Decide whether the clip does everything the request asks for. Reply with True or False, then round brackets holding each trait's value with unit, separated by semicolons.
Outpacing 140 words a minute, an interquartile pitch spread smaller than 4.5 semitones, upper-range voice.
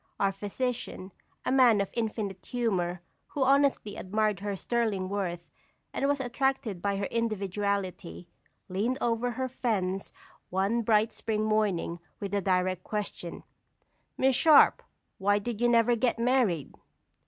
False (135 wpm; 3.9 semitones; 210 Hz)